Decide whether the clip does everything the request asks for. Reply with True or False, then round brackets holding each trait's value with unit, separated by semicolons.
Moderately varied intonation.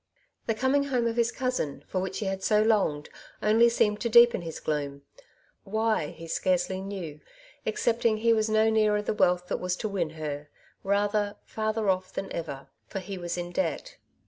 True (4.0 semitones)